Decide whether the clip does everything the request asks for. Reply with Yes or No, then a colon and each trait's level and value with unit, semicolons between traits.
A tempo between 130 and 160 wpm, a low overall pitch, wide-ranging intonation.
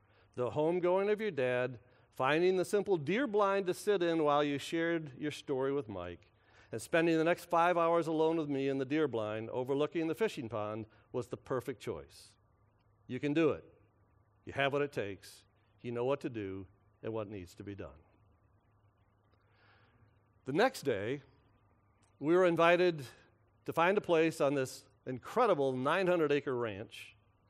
No: average, 170 wpm; low, 125 Hz; wide, 7.2 semitones